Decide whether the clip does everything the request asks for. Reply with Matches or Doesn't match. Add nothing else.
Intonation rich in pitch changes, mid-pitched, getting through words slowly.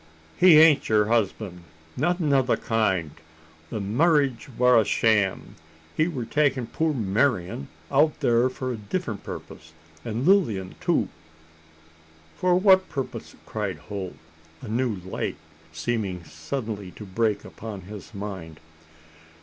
Doesn't match